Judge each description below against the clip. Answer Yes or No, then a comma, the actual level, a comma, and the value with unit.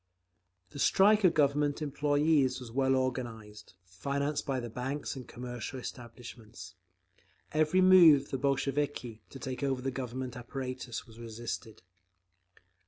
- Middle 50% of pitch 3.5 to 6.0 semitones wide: No, average, 3.1 semitones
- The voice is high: No, low, 130 Hz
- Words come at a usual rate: No, slow, 130 wpm